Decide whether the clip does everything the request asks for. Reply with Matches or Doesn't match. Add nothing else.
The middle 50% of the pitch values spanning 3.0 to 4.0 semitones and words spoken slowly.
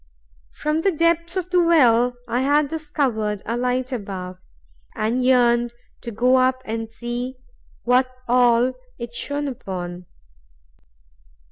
Matches